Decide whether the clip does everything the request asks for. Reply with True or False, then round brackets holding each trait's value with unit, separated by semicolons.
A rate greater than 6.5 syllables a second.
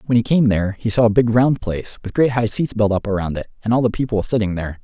True (6.8 syllables/s)